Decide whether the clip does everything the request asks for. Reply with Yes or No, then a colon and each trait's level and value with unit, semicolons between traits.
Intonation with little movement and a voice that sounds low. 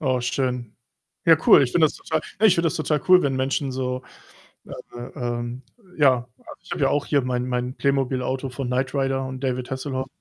Yes: narrow, 1.9 semitones; low, 130 Hz